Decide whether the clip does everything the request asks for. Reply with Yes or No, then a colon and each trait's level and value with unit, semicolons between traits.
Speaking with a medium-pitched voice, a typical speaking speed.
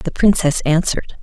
Yes: medium, 170 Hz; average, 145 wpm